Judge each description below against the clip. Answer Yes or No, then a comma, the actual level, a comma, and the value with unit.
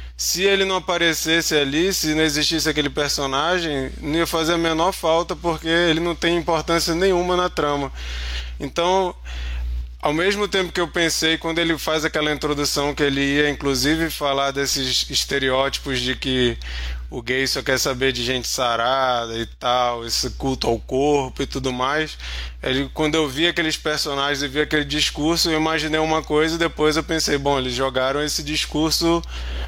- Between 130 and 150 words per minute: No, average, 170 wpm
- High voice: No, medium, 150 Hz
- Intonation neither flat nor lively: Yes, average, 3.7 semitones